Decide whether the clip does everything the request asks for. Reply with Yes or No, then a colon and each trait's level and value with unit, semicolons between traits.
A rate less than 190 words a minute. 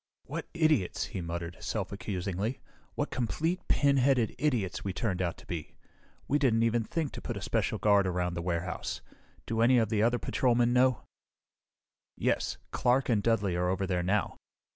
Yes: average, 170 wpm